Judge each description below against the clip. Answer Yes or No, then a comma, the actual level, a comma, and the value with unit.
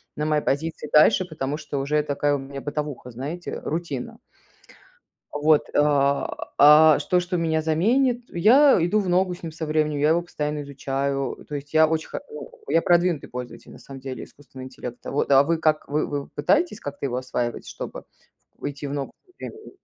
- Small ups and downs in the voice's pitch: No, average, 3.1 semitones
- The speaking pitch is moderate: Yes, medium, 150 Hz